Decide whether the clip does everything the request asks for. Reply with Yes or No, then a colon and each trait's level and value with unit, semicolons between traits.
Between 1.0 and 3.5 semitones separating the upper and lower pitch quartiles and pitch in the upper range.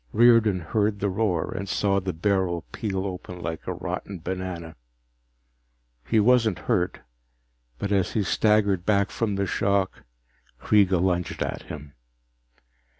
No: narrow, 2.4 semitones; very low, 95 Hz